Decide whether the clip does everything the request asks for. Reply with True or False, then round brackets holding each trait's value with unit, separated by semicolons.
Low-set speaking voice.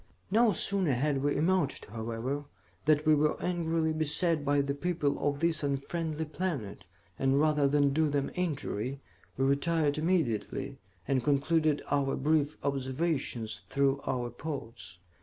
False (145 Hz)